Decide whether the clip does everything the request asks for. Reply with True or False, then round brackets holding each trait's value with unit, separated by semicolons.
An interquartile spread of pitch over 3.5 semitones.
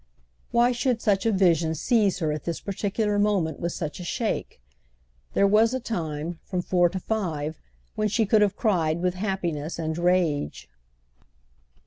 True (4.7 semitones)